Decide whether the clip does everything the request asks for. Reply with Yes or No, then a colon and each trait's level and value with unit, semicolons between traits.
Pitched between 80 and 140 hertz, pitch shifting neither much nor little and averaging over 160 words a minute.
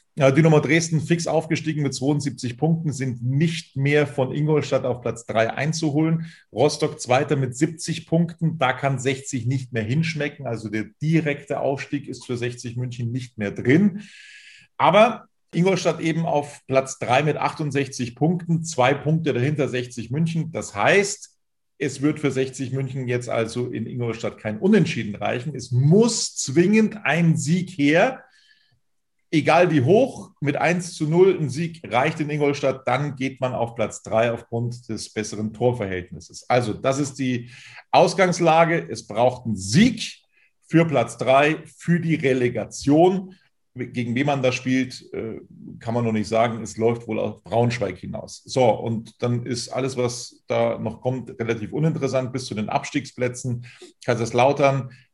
No: low, 135 Hz; average, 4.6 semitones; average, 155 wpm